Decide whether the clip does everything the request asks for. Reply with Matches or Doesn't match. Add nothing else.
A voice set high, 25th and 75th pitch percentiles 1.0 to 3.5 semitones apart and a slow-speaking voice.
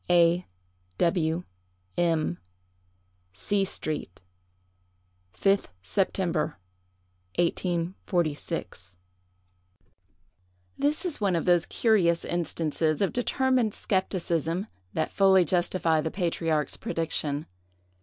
Doesn't match